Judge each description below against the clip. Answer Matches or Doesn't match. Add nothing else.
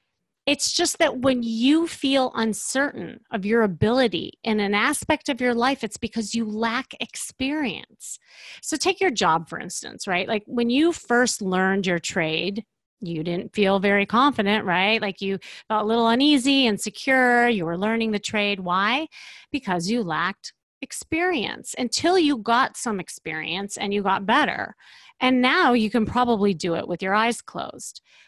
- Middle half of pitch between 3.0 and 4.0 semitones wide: Doesn't match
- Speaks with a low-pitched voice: Doesn't match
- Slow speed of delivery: Doesn't match